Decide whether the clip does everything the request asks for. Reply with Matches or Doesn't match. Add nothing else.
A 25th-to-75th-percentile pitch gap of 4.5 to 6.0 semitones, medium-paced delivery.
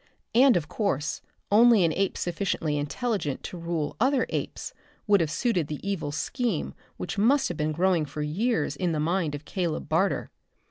Matches